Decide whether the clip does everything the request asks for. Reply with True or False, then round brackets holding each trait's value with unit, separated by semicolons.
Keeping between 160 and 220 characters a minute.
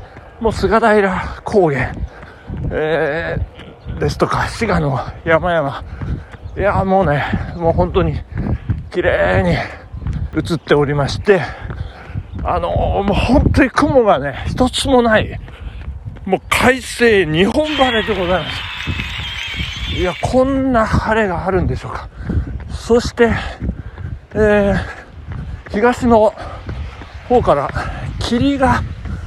True (195 characters per minute)